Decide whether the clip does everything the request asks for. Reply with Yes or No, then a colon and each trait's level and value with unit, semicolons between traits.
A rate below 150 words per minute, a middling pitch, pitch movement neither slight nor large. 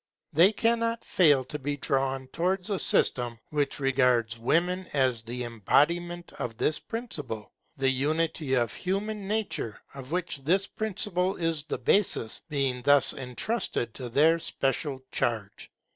No: average, 140 wpm; medium, 145 Hz; wide, 6.1 semitones